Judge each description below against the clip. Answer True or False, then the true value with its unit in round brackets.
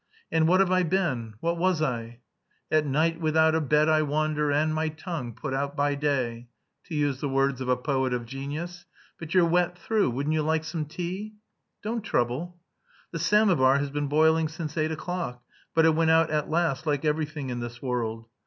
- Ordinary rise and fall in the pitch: True (3.3 semitones)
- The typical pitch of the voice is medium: True (155 Hz)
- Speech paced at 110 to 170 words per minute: False (200 wpm)